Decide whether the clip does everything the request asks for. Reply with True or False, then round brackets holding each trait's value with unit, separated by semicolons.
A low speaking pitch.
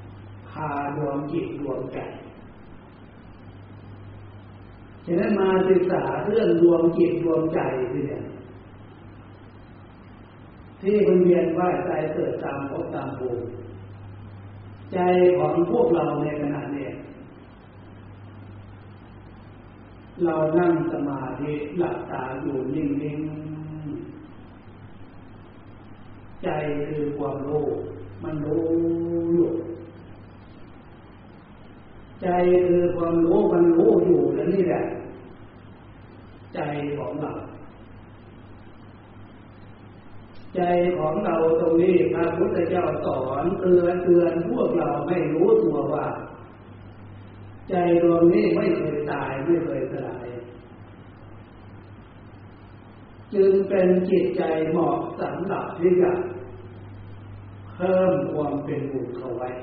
True (120 Hz)